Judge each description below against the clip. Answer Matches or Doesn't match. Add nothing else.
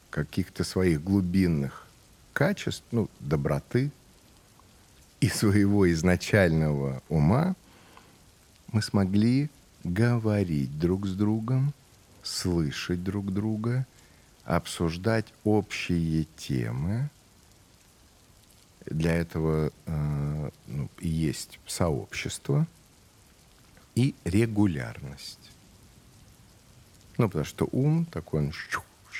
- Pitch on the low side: Matches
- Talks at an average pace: Doesn't match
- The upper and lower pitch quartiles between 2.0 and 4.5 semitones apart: Doesn't match